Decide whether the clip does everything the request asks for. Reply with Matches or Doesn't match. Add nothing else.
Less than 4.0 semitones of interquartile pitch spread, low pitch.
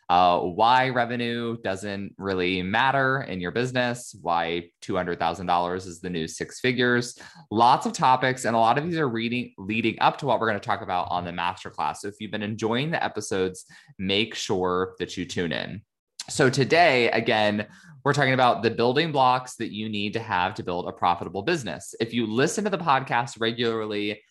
Doesn't match